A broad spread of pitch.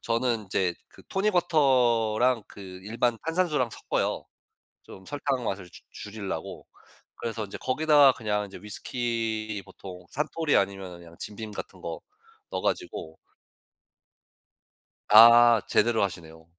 No: average, 4.5 semitones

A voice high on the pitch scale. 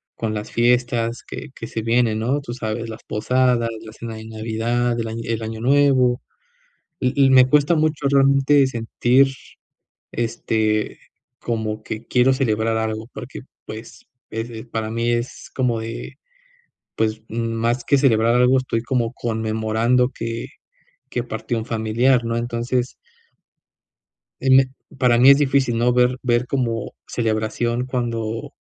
No: low, 120 Hz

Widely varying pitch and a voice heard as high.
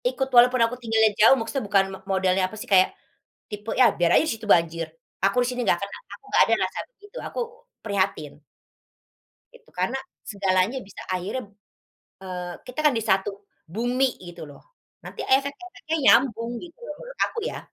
Yes: wide, 5.8 semitones; high, 220 Hz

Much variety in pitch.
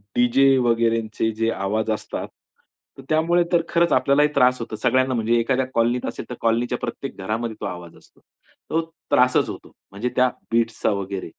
No: average, 2.8 semitones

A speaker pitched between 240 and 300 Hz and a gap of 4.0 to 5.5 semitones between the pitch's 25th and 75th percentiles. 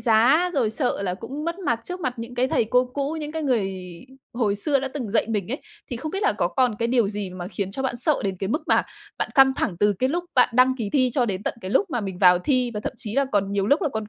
Yes: high, 245 Hz; average, 4.9 semitones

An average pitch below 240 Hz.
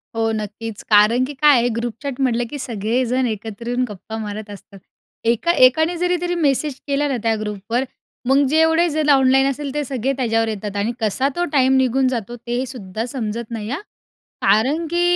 No: high, 245 Hz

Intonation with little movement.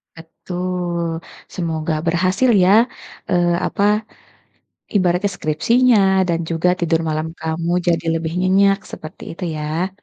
Yes: narrow, 2.2 semitones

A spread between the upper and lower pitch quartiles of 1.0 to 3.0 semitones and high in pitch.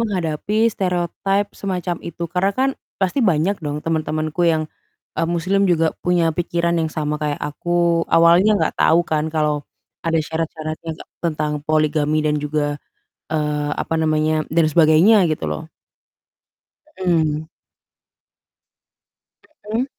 No: narrow, 2.4 semitones; medium, 160 Hz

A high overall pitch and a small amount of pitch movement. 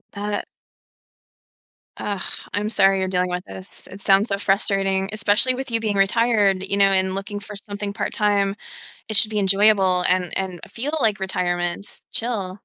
Yes: high, 200 Hz; narrow, 1.6 semitones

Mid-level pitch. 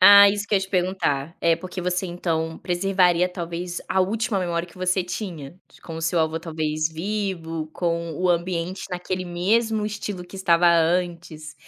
Yes: medium, 175 Hz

